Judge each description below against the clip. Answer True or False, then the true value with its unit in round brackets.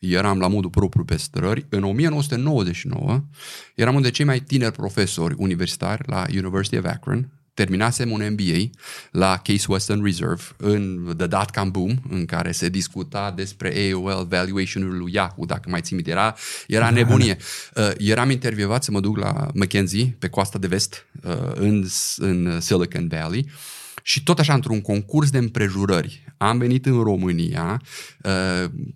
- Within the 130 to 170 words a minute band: True (160 wpm)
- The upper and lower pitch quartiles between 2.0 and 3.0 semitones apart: False (4.6 semitones)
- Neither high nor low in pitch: False (100 Hz)